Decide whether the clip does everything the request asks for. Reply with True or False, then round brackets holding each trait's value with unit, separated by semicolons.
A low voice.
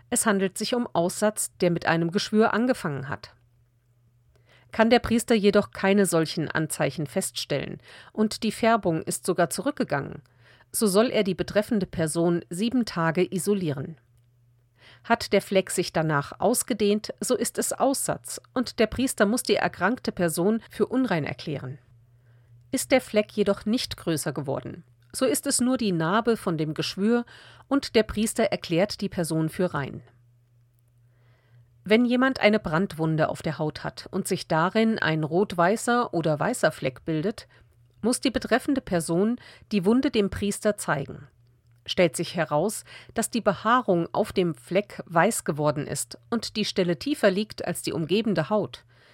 False (180 Hz)